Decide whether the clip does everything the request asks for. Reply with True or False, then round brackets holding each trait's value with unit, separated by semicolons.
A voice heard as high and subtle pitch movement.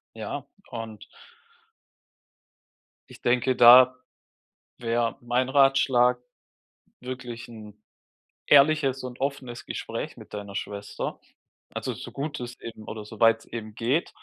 False (120 Hz; 2.3 semitones)